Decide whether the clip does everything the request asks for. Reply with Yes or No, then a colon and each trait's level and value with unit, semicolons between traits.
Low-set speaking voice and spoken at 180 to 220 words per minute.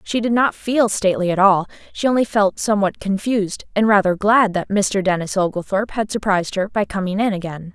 No: high, 200 Hz; average, 195 wpm